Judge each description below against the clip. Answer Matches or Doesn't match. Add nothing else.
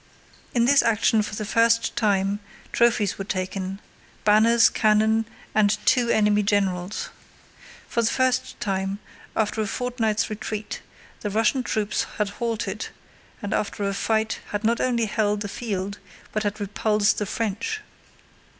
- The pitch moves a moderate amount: Doesn't match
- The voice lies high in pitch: Matches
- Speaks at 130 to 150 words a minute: Matches